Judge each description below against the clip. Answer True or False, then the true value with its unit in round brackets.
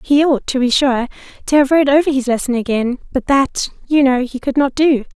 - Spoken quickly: True (230 wpm)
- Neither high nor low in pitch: False (265 Hz)